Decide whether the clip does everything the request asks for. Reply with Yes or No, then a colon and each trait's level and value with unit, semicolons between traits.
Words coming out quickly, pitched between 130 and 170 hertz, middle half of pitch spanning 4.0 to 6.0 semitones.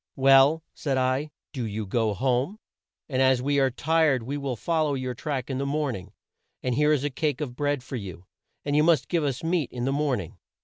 No: fast, 230 wpm; low, 135 Hz; average, 3.0 semitones